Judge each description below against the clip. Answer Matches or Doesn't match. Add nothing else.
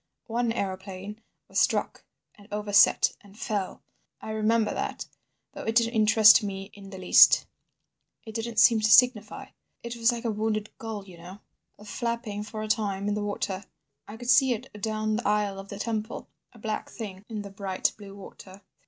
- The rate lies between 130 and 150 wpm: Doesn't match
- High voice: Matches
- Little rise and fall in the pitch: Matches